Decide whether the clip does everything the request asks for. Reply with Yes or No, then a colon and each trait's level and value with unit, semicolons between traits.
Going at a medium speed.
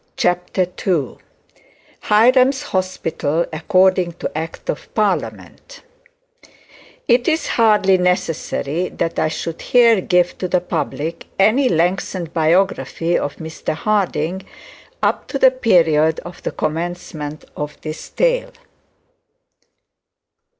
No: slow, 110 wpm